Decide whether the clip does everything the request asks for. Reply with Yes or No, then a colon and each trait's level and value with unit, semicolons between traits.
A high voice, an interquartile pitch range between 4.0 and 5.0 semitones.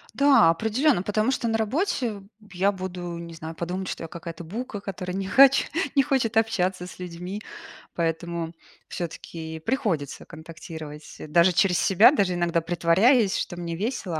No: medium, 180 Hz; average, 4.7 semitones